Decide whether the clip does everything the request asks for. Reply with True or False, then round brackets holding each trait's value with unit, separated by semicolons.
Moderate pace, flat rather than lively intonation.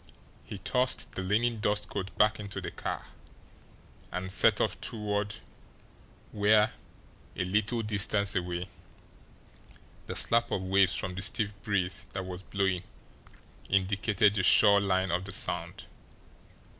False (130 wpm; 2.1 semitones)